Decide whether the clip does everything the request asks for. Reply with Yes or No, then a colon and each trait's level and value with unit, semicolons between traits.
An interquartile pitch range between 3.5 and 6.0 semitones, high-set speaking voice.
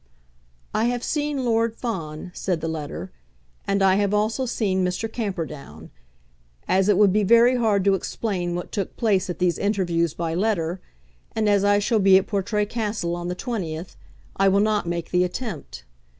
Yes: average, 3.8 semitones; high, 195 Hz